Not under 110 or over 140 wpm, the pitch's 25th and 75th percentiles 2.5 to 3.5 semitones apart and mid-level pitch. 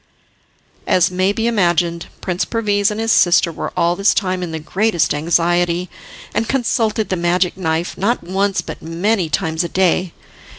No: average, 165 wpm; average, 3.1 semitones; medium, 180 Hz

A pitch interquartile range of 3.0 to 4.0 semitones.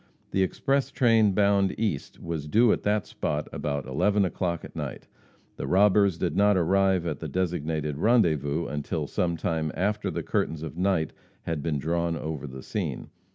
No: average, 4.6 semitones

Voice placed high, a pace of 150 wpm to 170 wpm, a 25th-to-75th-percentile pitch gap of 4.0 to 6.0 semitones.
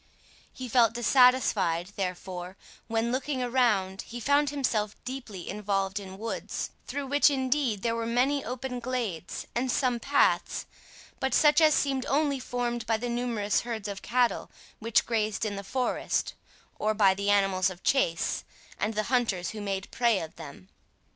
Yes: high, 230 Hz; average, 160 wpm; average, 4.4 semitones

